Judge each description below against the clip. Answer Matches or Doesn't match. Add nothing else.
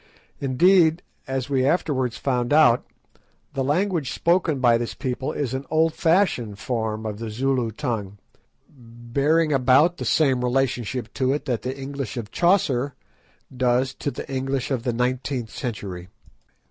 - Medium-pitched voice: Doesn't match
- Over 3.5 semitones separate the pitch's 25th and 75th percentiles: Doesn't match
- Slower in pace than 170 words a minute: Matches